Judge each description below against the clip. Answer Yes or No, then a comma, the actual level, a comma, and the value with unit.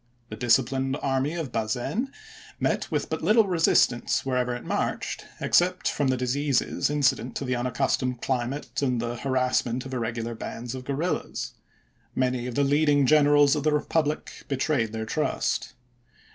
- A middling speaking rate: Yes, average, 155 wpm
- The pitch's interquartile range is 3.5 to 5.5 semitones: No, average, 3.1 semitones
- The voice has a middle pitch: No, low, 130 Hz